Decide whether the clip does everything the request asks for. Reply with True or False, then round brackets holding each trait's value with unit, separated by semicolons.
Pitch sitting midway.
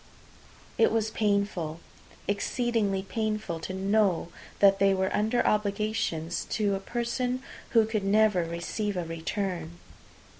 False (200 Hz)